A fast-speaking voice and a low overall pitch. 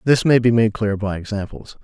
Yes: fast, 230 wpm; low, 110 Hz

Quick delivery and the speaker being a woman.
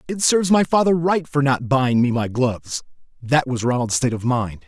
No: fast, 220 wpm; male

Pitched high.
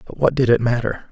No: low, 120 Hz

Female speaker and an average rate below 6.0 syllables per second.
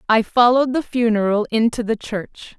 Yes: female; 5.1 syllables/s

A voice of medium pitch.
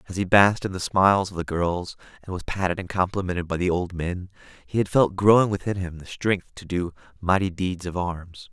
No: very low, 90 Hz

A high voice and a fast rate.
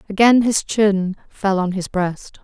No: high, 200 Hz; average, 175 wpm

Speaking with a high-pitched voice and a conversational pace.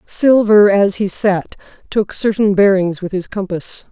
Yes: high, 200 Hz; average, 155 wpm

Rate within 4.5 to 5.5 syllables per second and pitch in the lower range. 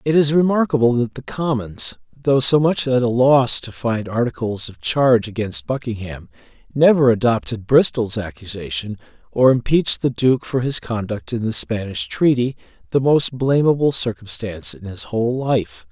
Yes: 4.8 syllables/s; low, 125 Hz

